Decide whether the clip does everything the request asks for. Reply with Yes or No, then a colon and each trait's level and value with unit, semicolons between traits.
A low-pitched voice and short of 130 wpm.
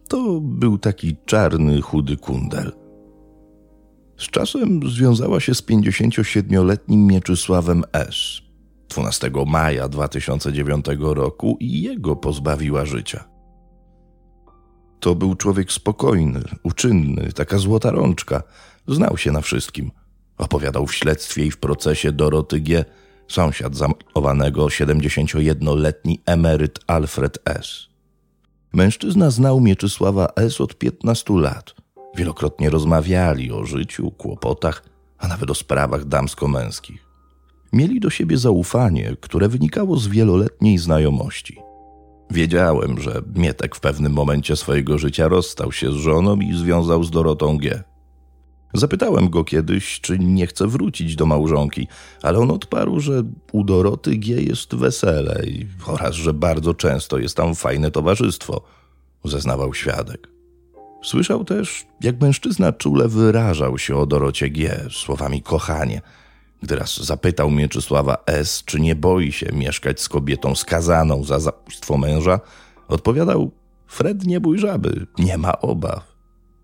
Yes: very low, 80 Hz; average, 120 wpm